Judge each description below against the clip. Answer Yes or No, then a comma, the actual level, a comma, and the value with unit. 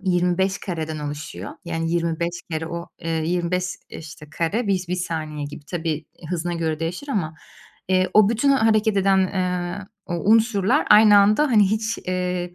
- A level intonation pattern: No, average, 3.5 semitones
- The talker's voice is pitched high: No, medium, 180 Hz